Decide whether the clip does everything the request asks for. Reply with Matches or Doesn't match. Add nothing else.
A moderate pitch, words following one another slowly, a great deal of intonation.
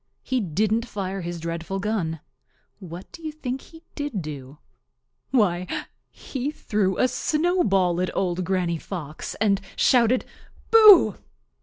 Doesn't match